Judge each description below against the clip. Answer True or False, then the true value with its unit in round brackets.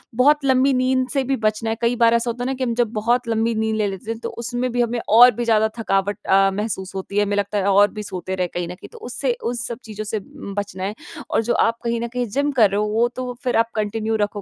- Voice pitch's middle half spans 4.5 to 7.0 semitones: False (3.0 semitones)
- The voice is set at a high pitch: True (225 Hz)